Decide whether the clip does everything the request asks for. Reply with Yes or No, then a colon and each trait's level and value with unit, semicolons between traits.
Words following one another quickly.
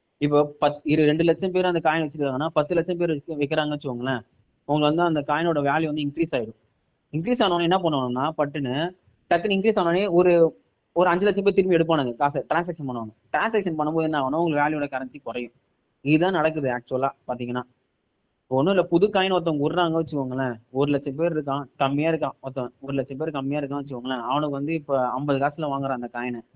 Yes: fast, 180 wpm